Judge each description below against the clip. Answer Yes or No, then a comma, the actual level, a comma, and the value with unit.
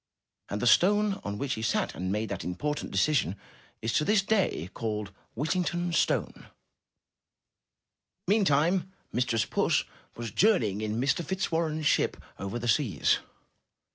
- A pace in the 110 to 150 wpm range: Yes, average, 140 wpm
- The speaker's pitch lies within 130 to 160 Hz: Yes, low, 135 Hz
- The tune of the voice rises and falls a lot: Yes, wide, 8.6 semitones